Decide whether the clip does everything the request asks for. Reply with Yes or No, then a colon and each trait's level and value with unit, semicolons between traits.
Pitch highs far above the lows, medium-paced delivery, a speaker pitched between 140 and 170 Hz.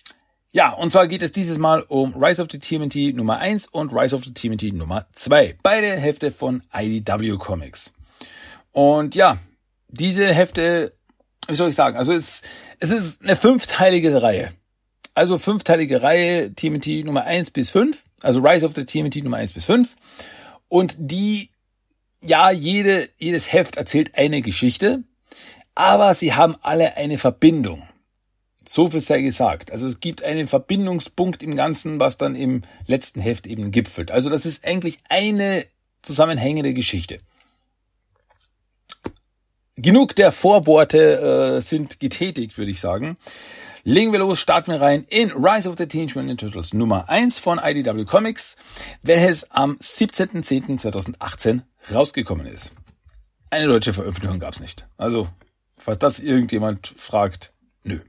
Yes: wide, 7.5 semitones; average, 145 wpm; medium, 150 Hz